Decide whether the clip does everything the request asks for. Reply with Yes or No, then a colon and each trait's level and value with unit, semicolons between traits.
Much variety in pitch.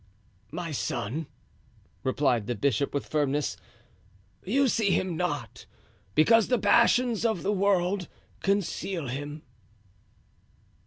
Yes: wide, 6.1 semitones